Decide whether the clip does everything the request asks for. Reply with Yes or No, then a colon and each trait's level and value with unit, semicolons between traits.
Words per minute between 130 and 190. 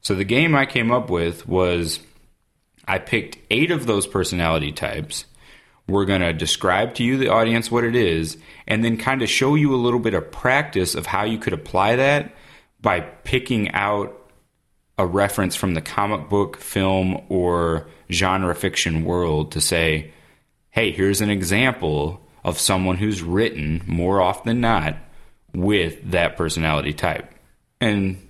Yes: average, 160 wpm